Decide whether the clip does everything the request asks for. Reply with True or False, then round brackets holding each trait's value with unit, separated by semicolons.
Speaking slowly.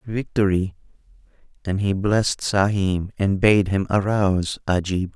True (115 wpm)